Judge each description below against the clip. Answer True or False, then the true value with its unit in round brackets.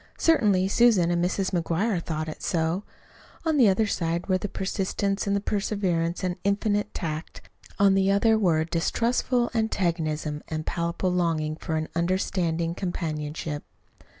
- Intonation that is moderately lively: True (3.4 semitones)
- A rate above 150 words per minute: False (145 wpm)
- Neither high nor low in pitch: True (180 Hz)